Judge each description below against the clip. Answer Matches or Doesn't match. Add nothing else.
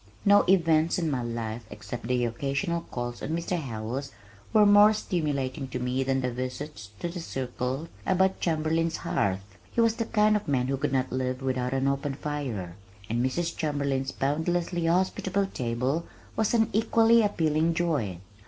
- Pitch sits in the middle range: Matches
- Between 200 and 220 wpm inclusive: Doesn't match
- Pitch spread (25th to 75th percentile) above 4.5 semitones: Matches